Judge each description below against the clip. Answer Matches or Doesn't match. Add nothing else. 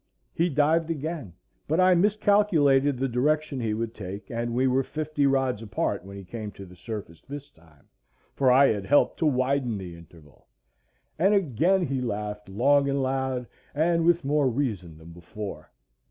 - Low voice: Matches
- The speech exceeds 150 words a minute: Matches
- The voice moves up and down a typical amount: Doesn't match